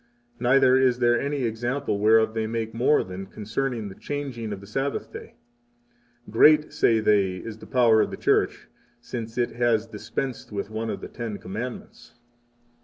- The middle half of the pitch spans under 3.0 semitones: Yes, narrow, 2.6 semitones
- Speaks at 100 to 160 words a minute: No, average, 170 wpm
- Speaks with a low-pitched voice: Yes, low, 115 Hz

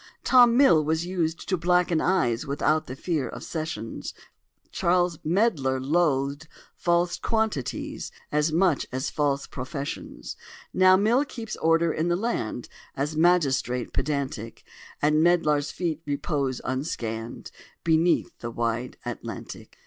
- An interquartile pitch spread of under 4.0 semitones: No, average, 4.5 semitones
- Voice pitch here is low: No, medium, 155 Hz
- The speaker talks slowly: Yes, slow, 125 wpm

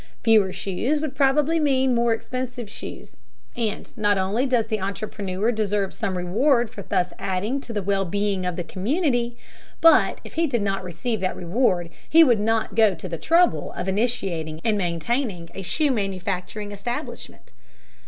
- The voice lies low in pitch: No, high, 215 Hz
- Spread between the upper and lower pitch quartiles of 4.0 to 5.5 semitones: Yes, average, 4.7 semitones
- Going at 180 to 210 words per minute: No, average, 165 wpm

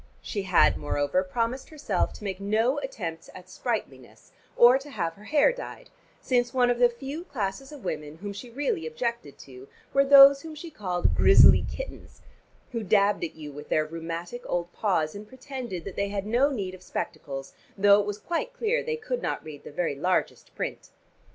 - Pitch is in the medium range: No, high, 205 Hz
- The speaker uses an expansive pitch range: Yes, wide, 7.6 semitones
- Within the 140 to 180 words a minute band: No, average, 190 wpm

